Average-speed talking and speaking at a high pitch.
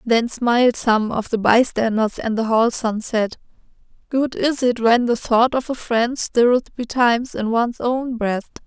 Yes: average, 180 wpm; high, 235 Hz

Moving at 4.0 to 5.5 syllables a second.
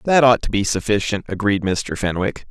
Yes: 5.2 syllables/s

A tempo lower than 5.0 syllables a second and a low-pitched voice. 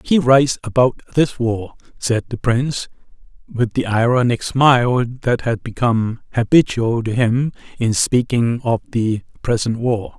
Yes: 4.4 syllables/s; low, 120 Hz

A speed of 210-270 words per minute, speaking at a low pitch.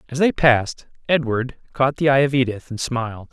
No: average, 200 wpm; low, 130 Hz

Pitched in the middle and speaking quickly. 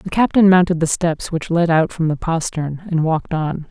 Yes: medium, 165 Hz; fast, 225 wpm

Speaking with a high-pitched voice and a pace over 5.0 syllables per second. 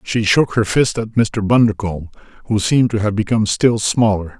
No: low, 110 Hz; 5.4 syllables/s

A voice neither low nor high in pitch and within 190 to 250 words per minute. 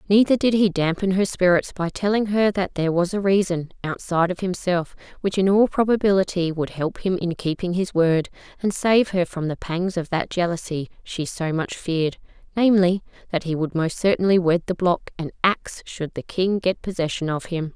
Yes: medium, 180 Hz; average, 200 wpm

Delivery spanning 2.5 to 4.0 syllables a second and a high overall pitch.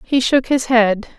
Yes: 3.9 syllables/s; high, 240 Hz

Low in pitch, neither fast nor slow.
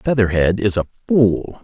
Yes: low, 110 Hz; average, 145 wpm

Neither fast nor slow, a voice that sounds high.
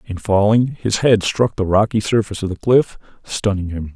No: average, 195 wpm; low, 105 Hz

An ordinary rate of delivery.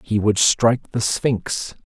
Yes: average, 160 wpm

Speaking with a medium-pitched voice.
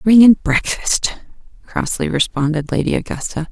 Yes: medium, 170 Hz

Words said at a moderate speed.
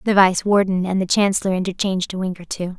No: fast, 235 wpm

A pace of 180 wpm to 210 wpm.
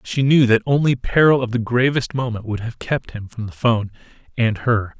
Yes: fast, 205 wpm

